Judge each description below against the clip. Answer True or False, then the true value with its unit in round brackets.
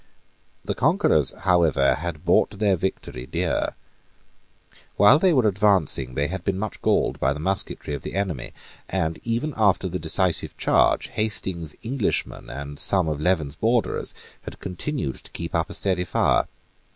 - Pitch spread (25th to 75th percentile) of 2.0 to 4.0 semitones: False (4.6 semitones)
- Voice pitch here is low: True (90 Hz)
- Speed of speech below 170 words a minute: True (155 wpm)